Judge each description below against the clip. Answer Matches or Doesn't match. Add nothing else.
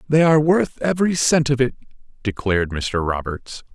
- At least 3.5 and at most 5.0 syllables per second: Doesn't match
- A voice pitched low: Matches